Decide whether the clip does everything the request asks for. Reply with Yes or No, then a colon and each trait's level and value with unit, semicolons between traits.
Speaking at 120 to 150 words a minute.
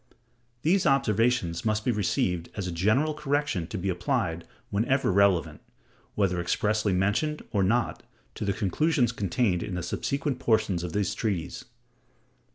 Yes: average, 145 wpm